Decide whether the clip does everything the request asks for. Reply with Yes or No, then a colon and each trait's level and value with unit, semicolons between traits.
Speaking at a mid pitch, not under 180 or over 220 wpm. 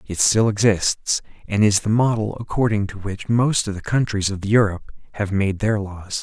No: low, 105 Hz; average, 195 wpm